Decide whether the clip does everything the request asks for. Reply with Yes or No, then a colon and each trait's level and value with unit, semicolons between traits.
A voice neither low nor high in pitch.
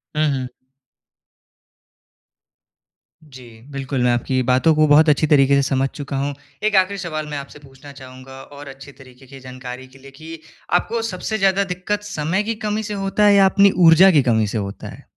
Yes: medium, 145 Hz